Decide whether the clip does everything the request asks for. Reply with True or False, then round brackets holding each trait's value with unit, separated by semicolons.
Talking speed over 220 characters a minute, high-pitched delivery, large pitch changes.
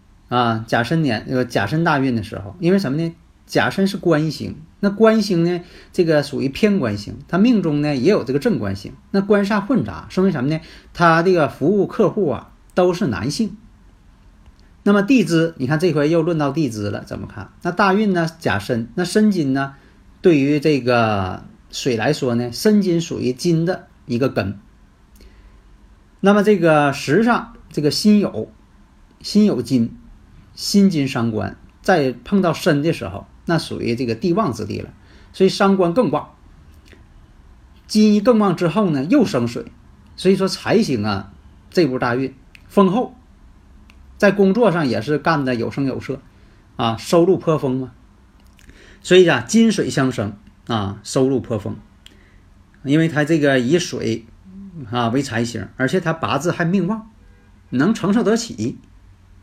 False (230 characters per minute; 140 Hz; 8.5 semitones)